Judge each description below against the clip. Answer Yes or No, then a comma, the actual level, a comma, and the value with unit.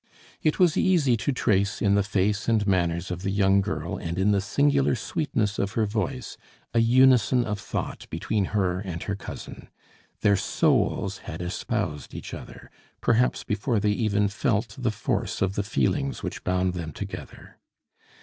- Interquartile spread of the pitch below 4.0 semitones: Yes, average, 3.6 semitones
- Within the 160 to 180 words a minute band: Yes, average, 170 wpm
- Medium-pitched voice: No, low, 105 Hz